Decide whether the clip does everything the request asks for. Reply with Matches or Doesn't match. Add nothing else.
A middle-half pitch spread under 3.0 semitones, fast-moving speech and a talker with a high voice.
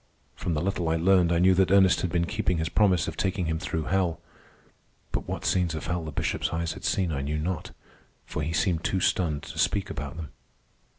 Doesn't match